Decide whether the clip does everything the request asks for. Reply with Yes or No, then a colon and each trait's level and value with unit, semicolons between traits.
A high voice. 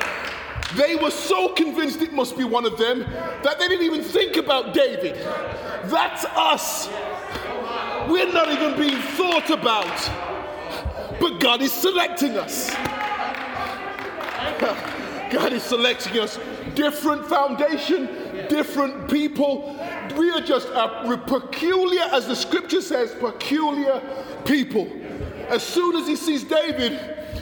Yes: very high, 300 Hz